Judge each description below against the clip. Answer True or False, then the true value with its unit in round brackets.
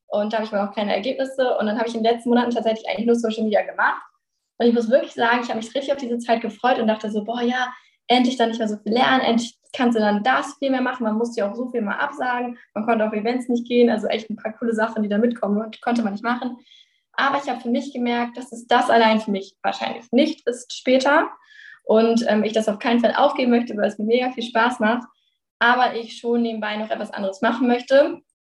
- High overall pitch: True (235 Hz)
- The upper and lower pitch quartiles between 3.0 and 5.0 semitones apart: False (2.4 semitones)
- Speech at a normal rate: False (255 wpm)